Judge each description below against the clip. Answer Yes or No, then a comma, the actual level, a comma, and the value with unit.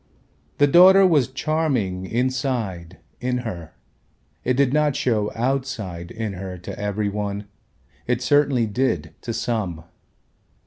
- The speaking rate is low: Yes, slow, 125 wpm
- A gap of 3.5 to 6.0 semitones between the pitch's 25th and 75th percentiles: Yes, average, 5.1 semitones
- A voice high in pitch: No, low, 120 Hz